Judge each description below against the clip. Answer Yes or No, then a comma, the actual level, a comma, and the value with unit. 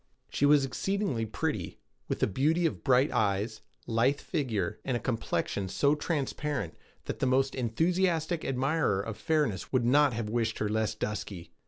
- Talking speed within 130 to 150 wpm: No, average, 160 wpm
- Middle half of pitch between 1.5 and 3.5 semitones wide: No, average, 5.2 semitones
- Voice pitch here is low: Yes, low, 130 Hz